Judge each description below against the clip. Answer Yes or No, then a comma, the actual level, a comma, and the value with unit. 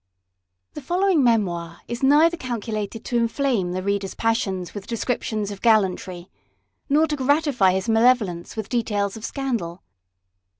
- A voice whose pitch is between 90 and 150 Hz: No, high, 225 Hz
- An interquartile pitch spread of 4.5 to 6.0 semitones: Yes, average, 5.1 semitones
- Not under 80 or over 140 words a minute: Yes, slow, 135 wpm